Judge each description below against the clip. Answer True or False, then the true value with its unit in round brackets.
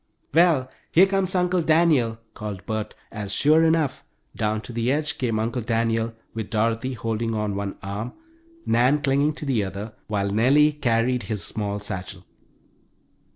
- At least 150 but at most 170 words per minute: True (155 wpm)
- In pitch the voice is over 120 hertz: False (115 Hz)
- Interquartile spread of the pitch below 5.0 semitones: False (5.5 semitones)